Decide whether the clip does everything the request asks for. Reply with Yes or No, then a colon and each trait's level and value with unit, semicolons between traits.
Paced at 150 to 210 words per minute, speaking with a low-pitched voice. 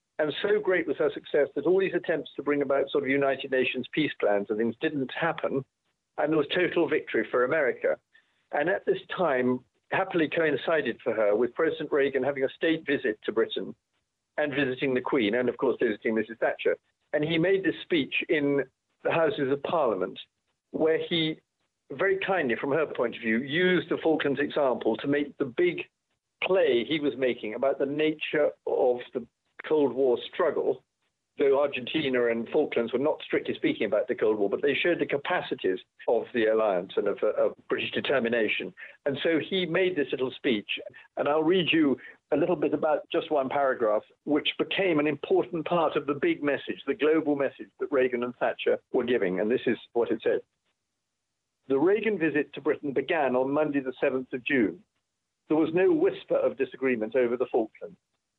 No: average, 190 wpm; medium, 160 Hz